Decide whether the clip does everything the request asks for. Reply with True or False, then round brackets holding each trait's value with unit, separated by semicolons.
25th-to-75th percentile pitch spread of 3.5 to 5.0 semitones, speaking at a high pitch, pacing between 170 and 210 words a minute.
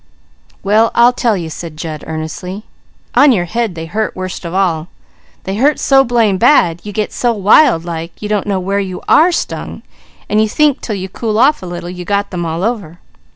True (4.7 semitones; 200 Hz; 205 wpm)